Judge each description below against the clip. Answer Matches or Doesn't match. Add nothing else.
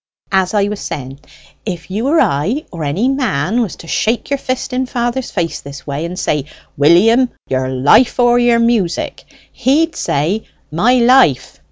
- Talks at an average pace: Matches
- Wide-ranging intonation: Matches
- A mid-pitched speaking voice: Doesn't match